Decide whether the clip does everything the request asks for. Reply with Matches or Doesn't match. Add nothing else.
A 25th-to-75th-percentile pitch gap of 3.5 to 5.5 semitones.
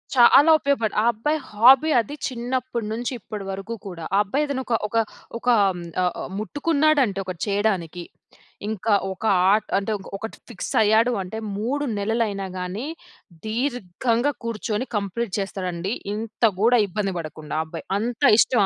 Matches